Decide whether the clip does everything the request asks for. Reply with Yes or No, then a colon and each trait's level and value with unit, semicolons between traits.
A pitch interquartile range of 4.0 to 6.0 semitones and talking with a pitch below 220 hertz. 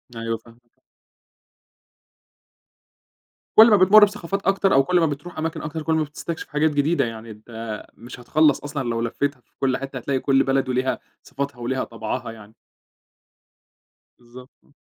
Yes: average, 4.9 semitones; low, 135 Hz